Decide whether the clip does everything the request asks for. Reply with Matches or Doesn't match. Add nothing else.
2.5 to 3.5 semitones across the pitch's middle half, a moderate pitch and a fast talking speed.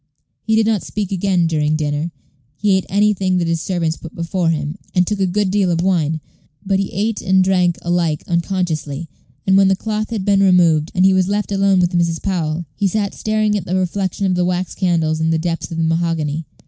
Matches